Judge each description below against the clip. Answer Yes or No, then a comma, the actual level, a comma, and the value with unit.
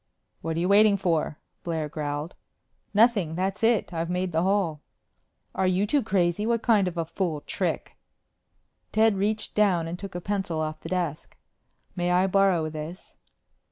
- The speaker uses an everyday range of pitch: Yes, average, 3.5 semitones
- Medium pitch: Yes, medium, 180 Hz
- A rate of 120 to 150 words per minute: No, average, 170 wpm